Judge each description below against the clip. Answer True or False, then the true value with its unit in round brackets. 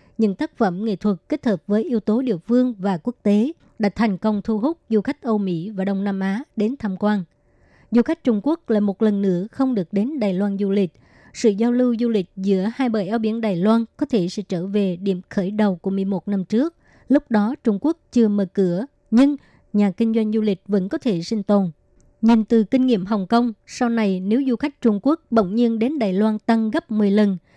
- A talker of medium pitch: False (215 Hz)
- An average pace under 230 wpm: False (240 wpm)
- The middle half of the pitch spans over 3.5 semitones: False (2.9 semitones)